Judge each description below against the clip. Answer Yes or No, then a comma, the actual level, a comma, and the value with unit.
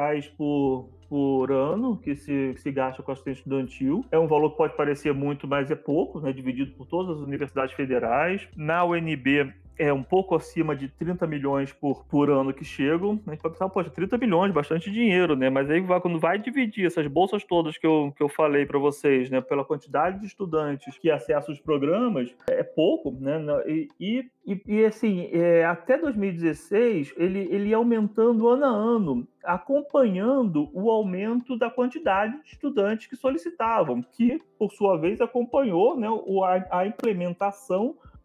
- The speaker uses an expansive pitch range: Yes, wide, 7.2 semitones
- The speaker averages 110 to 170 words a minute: No, average, 180 wpm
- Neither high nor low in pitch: Yes, medium, 170 Hz